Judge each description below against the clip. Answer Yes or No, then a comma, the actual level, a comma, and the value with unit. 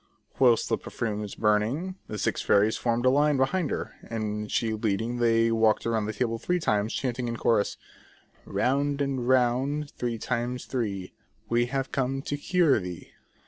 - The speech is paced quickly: No, average, 170 wpm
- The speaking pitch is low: Yes, low, 120 Hz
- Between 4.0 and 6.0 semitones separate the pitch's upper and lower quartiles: No, average, 3.6 semitones